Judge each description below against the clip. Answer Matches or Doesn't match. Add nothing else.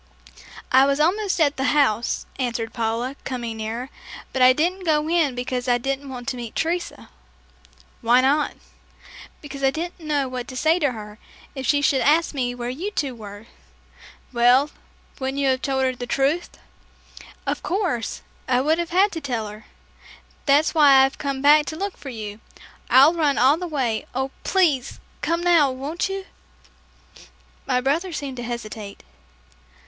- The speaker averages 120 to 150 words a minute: Doesn't match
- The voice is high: Matches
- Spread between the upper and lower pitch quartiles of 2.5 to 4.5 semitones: Matches